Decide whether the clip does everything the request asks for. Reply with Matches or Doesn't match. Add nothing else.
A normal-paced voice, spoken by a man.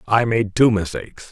Matches